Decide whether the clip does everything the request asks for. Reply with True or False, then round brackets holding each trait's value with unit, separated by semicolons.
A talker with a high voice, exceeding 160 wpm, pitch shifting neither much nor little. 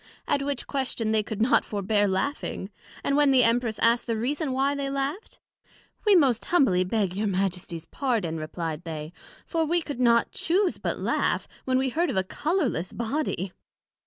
False (235 Hz; 175 wpm; 6.5 semitones)